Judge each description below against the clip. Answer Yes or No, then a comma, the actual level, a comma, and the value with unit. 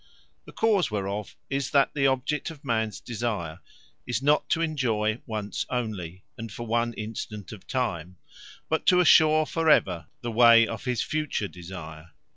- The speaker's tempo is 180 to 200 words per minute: No, average, 160 wpm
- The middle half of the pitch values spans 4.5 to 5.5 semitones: Yes, average, 5.2 semitones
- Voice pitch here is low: Yes, low, 115 Hz